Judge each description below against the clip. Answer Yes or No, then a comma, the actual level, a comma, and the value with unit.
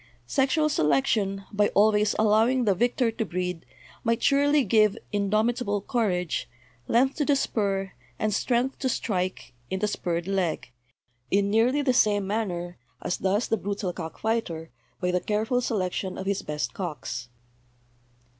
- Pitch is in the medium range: No, high, 205 Hz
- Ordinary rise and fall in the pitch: Yes, average, 4.1 semitones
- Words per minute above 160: No, average, 145 wpm